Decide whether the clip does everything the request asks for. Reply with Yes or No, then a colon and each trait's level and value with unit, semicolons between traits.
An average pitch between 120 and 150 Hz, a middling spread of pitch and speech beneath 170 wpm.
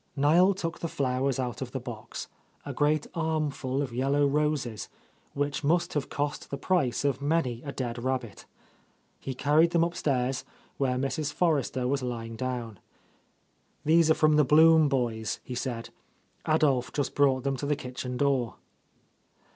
Yes: medium, 140 Hz; average, 3.3 semitones; average, 155 wpm